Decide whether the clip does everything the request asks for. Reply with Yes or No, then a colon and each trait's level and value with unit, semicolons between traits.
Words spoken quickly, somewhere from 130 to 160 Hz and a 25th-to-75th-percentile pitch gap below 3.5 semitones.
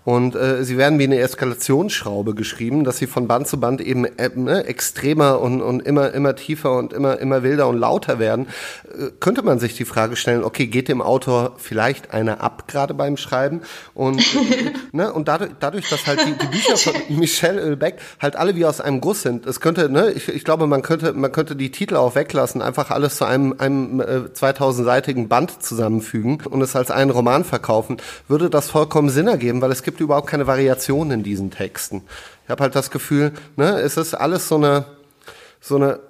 Yes: fast, 205 wpm; low, 135 Hz; average, 2.8 semitones